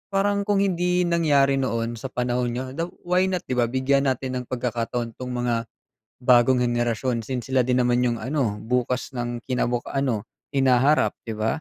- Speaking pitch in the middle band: No, low, 125 Hz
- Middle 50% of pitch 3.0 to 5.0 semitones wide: No, narrow, 2.4 semitones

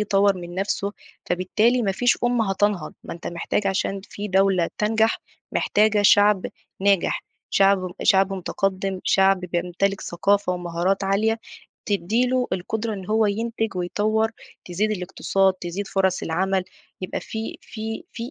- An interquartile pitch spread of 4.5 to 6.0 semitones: No, narrow, 2.5 semitones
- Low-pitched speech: No, high, 195 Hz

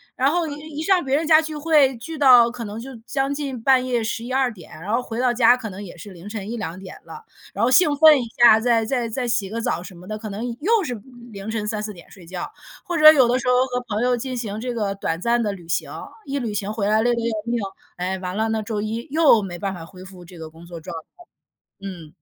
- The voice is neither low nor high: No, high, 230 Hz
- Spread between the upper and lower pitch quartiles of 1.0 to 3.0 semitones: No, average, 4.5 semitones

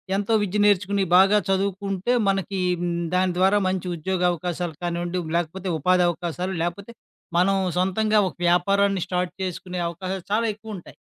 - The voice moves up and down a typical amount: No, narrow, 2.0 semitones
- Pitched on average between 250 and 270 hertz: No, medium, 185 Hz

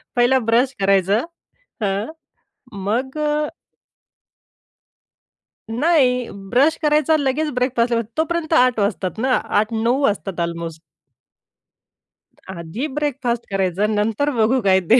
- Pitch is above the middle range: Yes, high, 235 Hz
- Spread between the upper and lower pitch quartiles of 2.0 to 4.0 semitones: No, average, 4.8 semitones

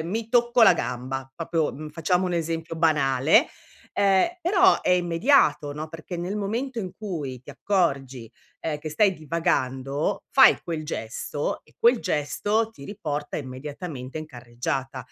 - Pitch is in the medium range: Yes, medium, 160 Hz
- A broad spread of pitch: Yes, wide, 6.1 semitones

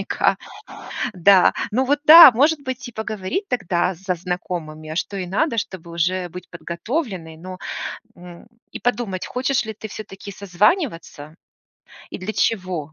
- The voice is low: No, high, 190 Hz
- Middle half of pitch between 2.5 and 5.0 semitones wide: No, wide, 5.5 semitones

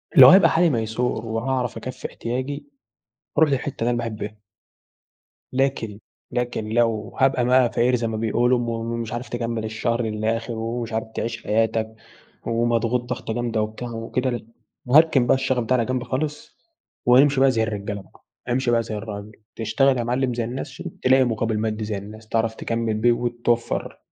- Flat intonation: Yes, narrow, 2.1 semitones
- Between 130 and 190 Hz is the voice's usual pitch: No, low, 120 Hz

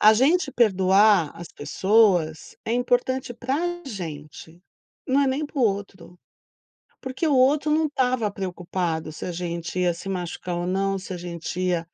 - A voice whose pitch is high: Yes, high, 195 Hz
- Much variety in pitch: Yes, wide, 6.4 semitones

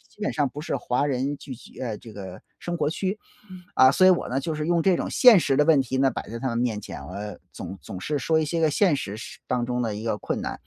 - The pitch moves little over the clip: No, average, 5.3 semitones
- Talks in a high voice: No, low, 135 Hz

